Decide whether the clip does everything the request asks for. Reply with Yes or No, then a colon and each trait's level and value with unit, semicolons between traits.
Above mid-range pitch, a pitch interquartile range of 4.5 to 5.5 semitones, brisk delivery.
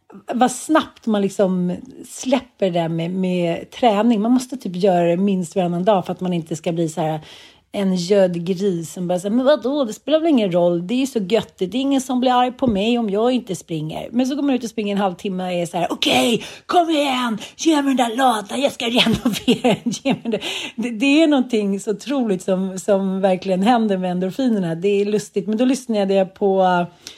Yes: high, 210 Hz; average, 5.2 semitones; fast, 225 wpm